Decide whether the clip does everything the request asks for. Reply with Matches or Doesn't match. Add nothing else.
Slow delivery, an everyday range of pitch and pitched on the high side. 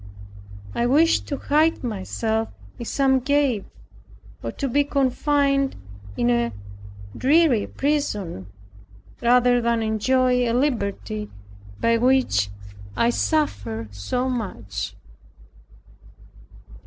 Matches